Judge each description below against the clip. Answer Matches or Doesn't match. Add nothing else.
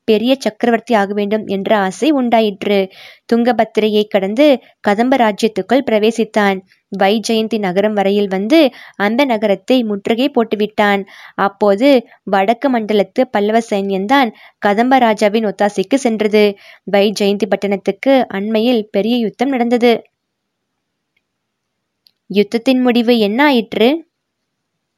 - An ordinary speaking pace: Matches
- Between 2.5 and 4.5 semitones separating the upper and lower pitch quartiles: Matches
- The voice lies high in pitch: Matches